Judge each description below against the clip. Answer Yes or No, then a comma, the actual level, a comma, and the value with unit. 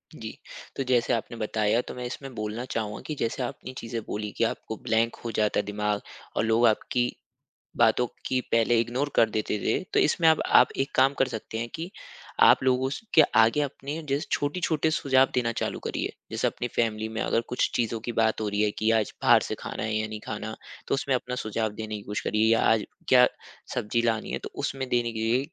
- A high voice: No, low, 115 Hz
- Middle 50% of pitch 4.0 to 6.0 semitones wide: No, average, 2.9 semitones